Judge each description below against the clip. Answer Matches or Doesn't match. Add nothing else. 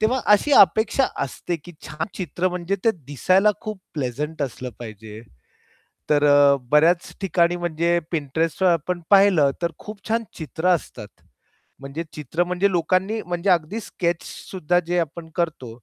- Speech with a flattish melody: Doesn't match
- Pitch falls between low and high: Matches